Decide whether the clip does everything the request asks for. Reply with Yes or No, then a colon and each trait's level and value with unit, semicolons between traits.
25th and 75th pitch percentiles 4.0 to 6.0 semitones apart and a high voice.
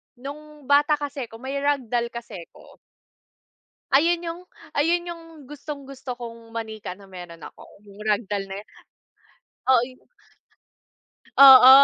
Yes: average, 4.7 semitones; very high, 260 Hz